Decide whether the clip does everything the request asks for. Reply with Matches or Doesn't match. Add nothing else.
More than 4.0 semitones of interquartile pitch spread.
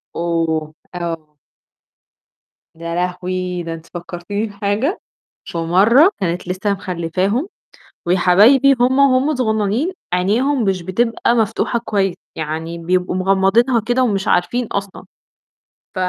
Matches